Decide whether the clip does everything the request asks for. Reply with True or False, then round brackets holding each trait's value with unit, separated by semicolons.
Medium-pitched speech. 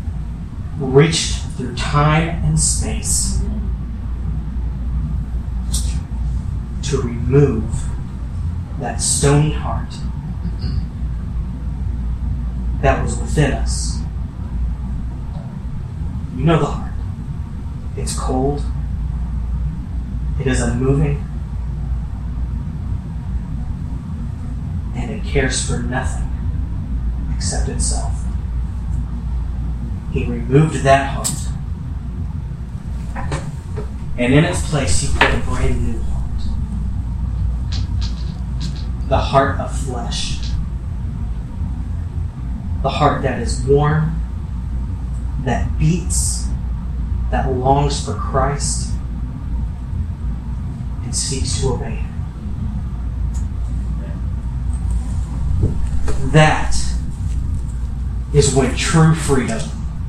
False (80 Hz)